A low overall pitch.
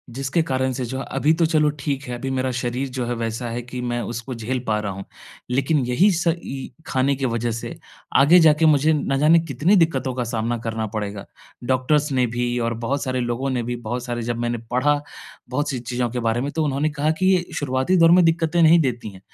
Yes: low, 130 Hz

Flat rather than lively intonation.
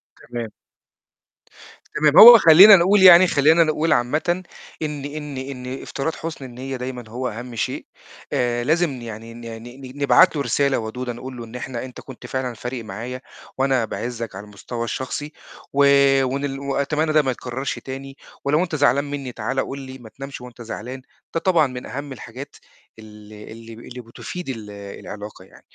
No: average, 3.4 semitones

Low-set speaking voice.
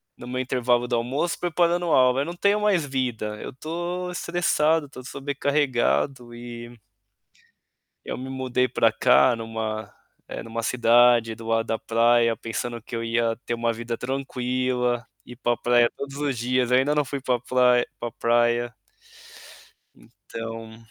Yes: low, 125 Hz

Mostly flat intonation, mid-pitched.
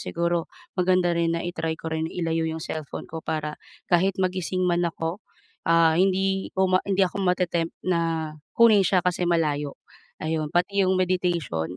Yes: narrow, 2.2 semitones; medium, 170 Hz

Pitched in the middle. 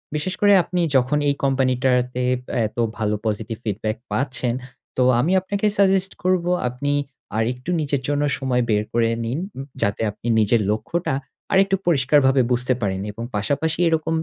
No: low, 130 Hz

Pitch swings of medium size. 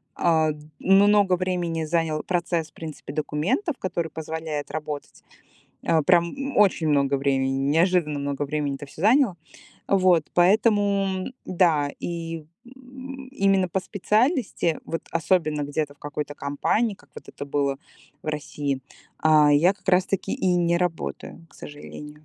Yes: average, 4.2 semitones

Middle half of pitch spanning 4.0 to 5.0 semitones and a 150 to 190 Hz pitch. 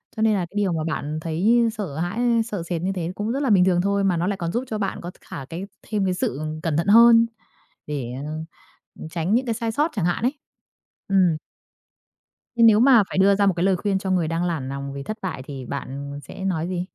Yes: average, 4.5 semitones; medium, 185 Hz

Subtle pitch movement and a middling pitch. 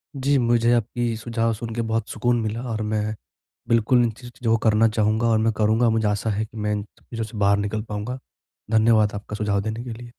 No: narrow, 1.7 semitones; low, 110 Hz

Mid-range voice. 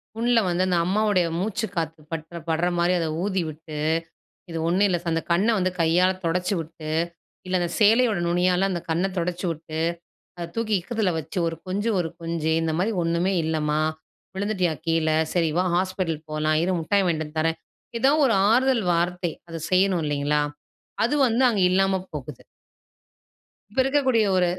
Yes: medium, 175 Hz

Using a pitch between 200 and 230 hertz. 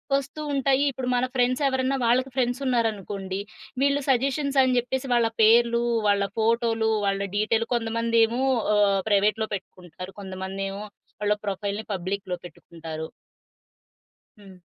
Yes: high, 225 Hz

